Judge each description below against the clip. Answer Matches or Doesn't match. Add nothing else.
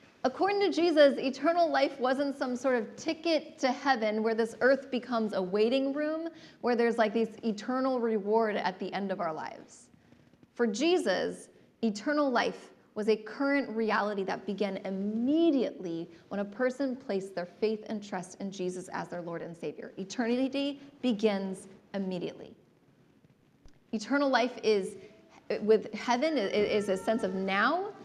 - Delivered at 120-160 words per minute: Matches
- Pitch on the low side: Doesn't match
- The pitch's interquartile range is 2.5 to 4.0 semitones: Doesn't match